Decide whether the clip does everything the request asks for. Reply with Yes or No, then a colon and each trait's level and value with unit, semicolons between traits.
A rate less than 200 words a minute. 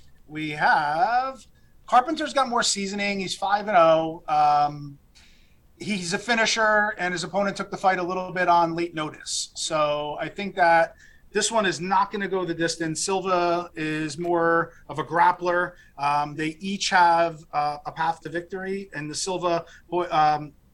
Yes: average, 170 wpm